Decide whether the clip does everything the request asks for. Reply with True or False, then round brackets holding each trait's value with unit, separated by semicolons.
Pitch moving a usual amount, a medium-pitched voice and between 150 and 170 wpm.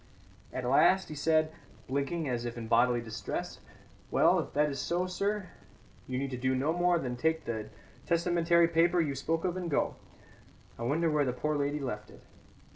False (5.0 semitones; 150 Hz; 185 wpm)